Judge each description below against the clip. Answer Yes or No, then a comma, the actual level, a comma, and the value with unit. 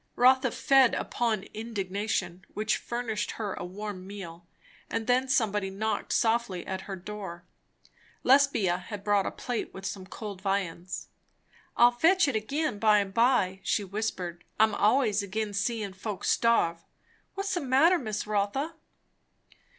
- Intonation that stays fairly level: No, average, 3.8 semitones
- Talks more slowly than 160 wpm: Yes, average, 145 wpm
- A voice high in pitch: Yes, high, 210 Hz